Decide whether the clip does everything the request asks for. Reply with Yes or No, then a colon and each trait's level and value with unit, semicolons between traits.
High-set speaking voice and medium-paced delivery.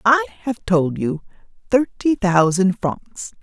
No: high, 195 Hz; slow, 125 wpm